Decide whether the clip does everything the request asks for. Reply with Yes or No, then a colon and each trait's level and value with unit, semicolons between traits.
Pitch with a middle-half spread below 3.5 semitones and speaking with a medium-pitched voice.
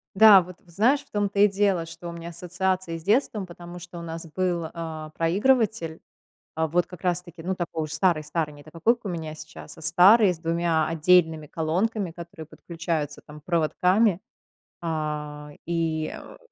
Yes: narrow, 2.5 semitones; medium, 170 Hz